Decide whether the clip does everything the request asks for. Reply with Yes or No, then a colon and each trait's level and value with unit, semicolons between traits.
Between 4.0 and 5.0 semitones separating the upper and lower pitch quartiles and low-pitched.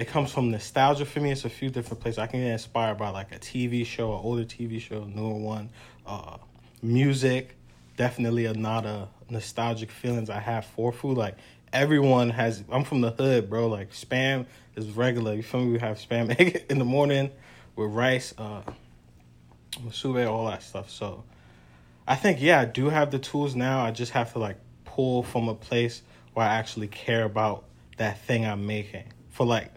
No: average, 2.8 semitones; low, 115 Hz